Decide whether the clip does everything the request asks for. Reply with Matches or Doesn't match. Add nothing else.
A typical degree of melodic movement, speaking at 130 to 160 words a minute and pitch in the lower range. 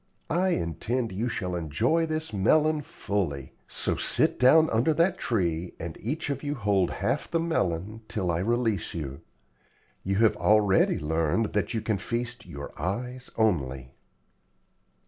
Doesn't match